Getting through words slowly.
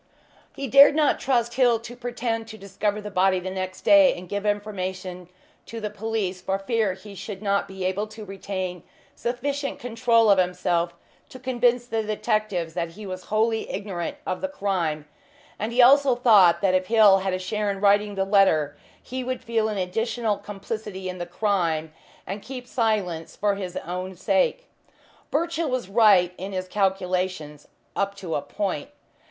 No: average, 175 wpm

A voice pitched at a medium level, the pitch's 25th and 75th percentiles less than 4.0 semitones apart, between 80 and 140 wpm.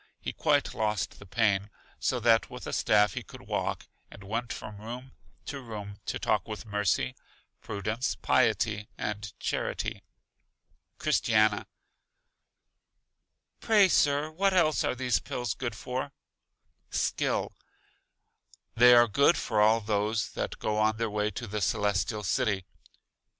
No: low, 110 Hz; average, 2.9 semitones; slow, 135 wpm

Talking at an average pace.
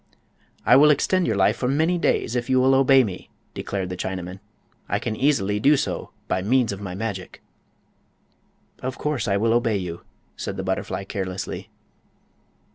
Yes: average, 170 wpm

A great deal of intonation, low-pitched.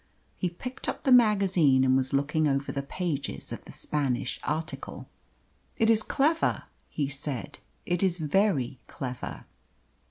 No: wide, 6.1 semitones; medium, 150 Hz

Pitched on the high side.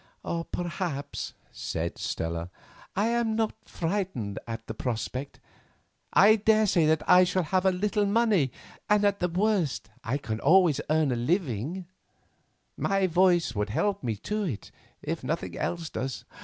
No: medium, 175 Hz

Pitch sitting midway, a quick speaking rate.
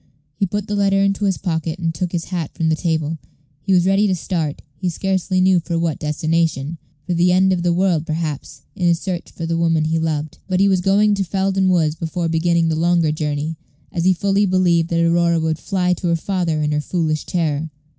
Yes: medium, 170 Hz; fast, 225 wpm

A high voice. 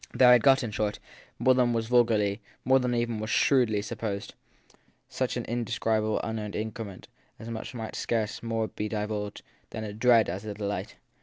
No: low, 110 Hz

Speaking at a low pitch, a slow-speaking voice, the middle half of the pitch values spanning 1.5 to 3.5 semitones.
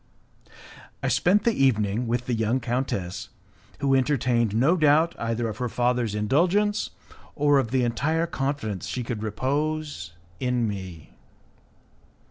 No: low, 125 Hz; slow, 130 wpm; average, 4.6 semitones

